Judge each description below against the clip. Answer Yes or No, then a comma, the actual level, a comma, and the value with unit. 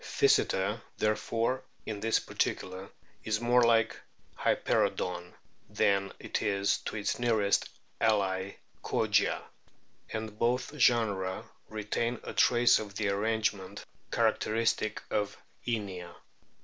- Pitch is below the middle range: Yes, low, 105 Hz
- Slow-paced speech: Yes, slow, 110 wpm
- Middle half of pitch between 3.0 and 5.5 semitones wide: No, narrow, 2.6 semitones